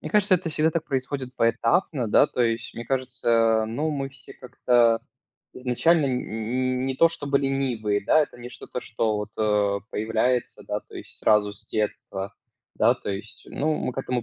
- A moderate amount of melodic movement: Yes, average, 3.8 semitones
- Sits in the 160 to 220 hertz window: No, low, 125 Hz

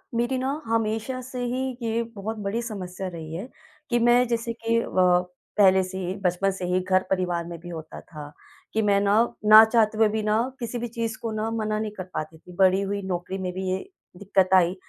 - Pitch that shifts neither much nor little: Yes, average, 3.6 semitones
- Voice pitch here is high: Yes, high, 205 Hz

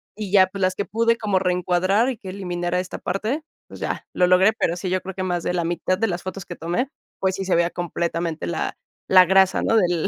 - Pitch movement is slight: Yes, narrow, 1.9 semitones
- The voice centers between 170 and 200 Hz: Yes, medium, 185 Hz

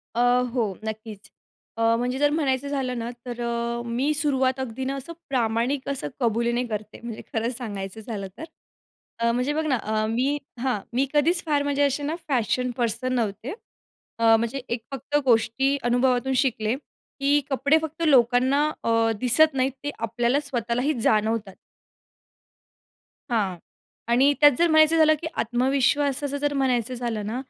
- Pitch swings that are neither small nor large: Yes, average, 3.5 semitones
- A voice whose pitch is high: Yes, very high, 250 Hz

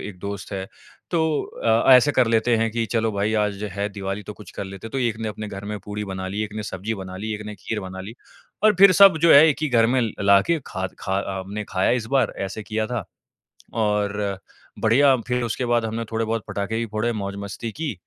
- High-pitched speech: No, low, 110 Hz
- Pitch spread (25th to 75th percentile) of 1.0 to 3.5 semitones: Yes, average, 2.7 semitones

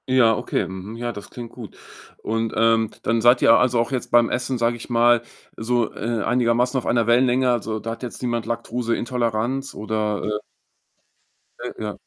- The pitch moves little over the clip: Yes, narrow, 1.5 semitones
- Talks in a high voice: No, low, 115 Hz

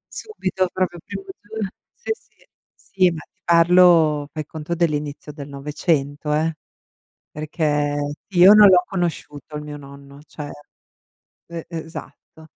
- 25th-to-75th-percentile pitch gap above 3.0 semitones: Yes, average, 3.4 semitones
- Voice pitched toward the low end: No, medium, 160 Hz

